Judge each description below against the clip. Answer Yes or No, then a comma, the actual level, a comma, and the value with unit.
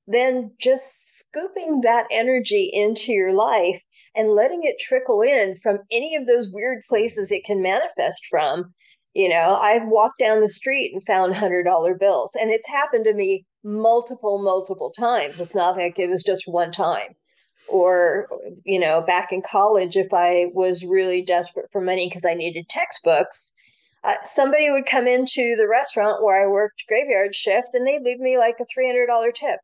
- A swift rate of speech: No, average, 175 wpm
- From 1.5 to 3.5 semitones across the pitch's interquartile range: No, wide, 5.5 semitones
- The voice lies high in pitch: Yes, high, 215 Hz